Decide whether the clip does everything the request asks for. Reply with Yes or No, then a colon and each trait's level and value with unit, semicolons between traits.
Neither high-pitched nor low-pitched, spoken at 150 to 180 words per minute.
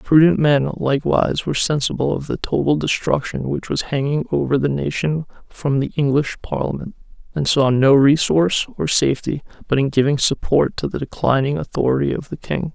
Yes: medium, 145 Hz; average, 170 wpm